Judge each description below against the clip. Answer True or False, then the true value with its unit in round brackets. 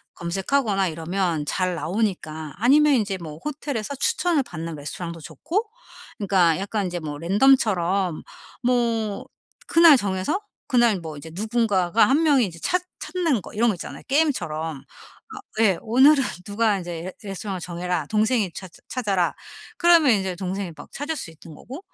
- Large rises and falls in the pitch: True (6.6 semitones)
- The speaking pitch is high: True (200 Hz)